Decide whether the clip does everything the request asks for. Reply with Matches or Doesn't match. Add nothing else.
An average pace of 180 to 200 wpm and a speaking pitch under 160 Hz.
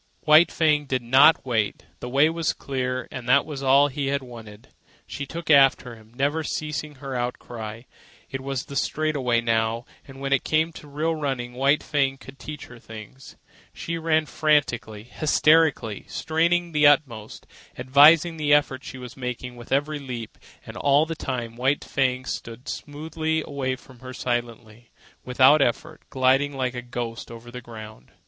Doesn't match